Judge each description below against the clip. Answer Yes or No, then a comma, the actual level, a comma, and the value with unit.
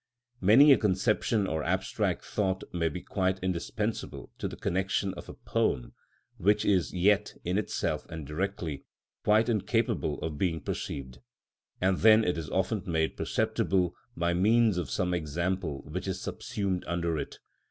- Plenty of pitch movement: No, average, 3.4 semitones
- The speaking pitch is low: Yes, very low, 90 Hz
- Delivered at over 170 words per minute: No, average, 150 wpm